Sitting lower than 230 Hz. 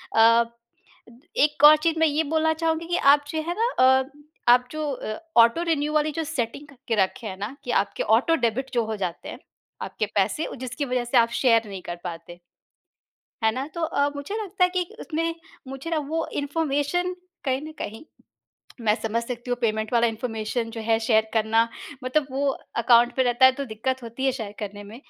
No: very high, 255 Hz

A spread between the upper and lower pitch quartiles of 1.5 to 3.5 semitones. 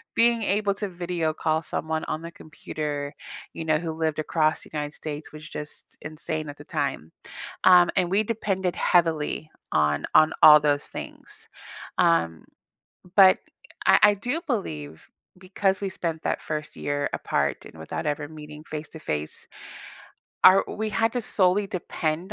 No: average, 3.9 semitones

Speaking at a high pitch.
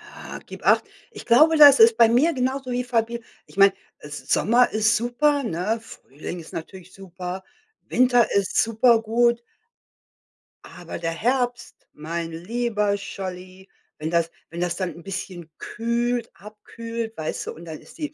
Yes: high, 220 Hz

